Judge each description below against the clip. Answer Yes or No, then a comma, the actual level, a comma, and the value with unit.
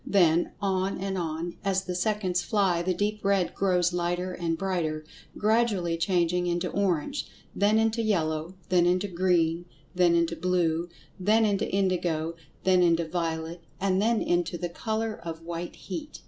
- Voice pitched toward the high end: No, medium, 180 Hz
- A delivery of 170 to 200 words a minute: No, average, 155 wpm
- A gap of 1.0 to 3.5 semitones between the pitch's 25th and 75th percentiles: Yes, narrow, 2.6 semitones